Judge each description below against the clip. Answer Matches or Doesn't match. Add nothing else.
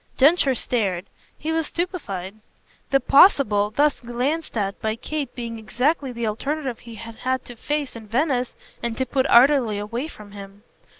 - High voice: Matches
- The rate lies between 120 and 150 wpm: Doesn't match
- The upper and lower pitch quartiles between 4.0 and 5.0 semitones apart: Matches